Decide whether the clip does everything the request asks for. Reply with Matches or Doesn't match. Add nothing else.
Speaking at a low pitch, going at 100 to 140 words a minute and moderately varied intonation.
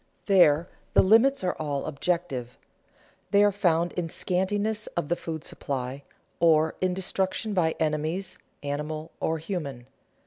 Doesn't match